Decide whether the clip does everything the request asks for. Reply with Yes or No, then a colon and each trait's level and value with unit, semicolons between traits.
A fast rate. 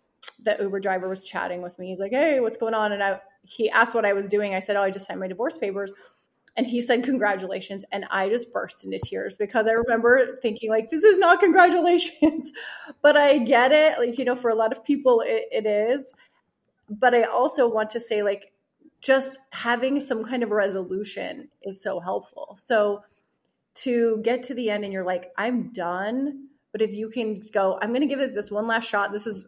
Yes: fast, 215 wpm